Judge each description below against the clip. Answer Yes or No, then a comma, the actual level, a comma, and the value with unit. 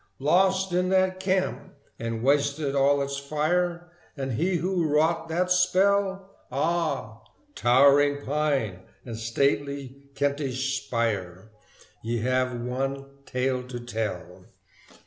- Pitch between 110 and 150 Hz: Yes, medium, 140 Hz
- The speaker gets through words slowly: Yes, slow, 110 wpm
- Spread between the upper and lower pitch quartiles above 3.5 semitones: Yes, wide, 5.5 semitones